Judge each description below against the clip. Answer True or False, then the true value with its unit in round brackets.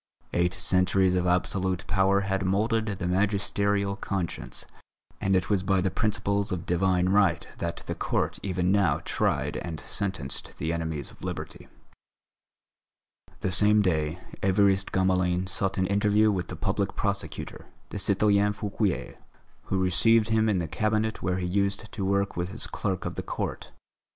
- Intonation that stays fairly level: True (1.9 semitones)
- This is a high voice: False (95 Hz)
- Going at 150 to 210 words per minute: True (155 wpm)